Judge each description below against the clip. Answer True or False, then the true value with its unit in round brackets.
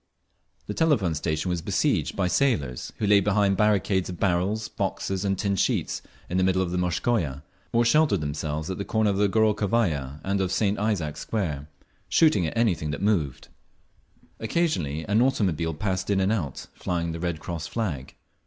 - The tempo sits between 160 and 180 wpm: True (175 wpm)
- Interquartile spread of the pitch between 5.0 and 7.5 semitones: False (4.5 semitones)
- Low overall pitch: True (95 Hz)